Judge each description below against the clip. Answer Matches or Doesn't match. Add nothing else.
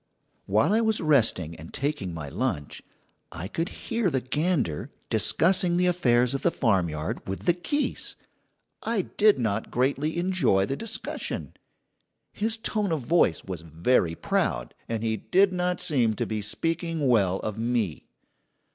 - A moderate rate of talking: Matches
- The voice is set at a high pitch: Doesn't match